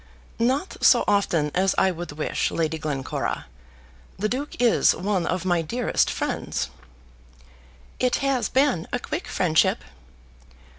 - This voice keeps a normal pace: No, slow, 130 wpm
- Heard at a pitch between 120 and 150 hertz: No, high, 190 Hz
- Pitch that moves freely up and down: Yes, wide, 7.0 semitones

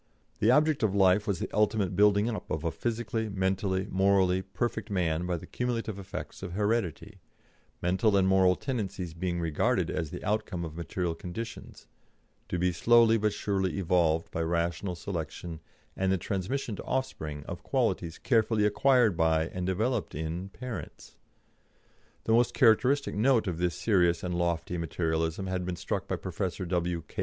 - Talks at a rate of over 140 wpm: Yes, average, 165 wpm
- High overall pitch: No, very low, 95 Hz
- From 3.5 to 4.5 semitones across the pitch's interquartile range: Yes, average, 3.9 semitones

